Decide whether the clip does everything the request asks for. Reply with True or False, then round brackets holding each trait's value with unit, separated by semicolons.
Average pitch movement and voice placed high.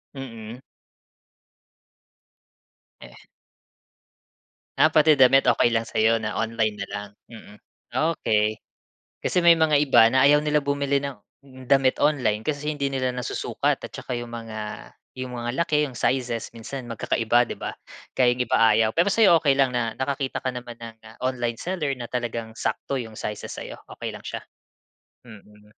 False (3.6 semitones; 125 Hz)